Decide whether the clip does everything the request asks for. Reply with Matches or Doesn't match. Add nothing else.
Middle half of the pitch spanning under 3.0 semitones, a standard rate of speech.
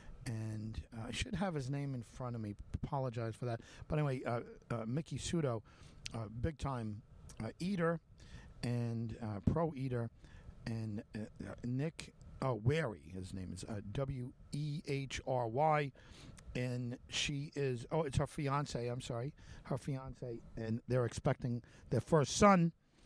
Doesn't match